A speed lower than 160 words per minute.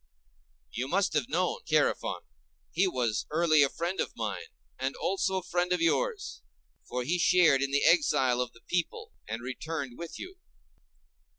No: average, 165 wpm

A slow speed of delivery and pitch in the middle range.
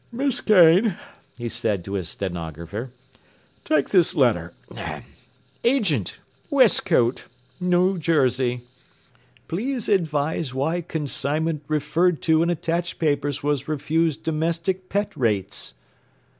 Yes: slow, 100 wpm; medium, 155 Hz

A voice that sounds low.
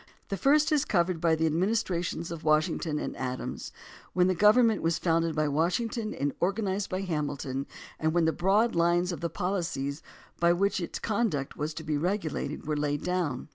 No: medium, 170 Hz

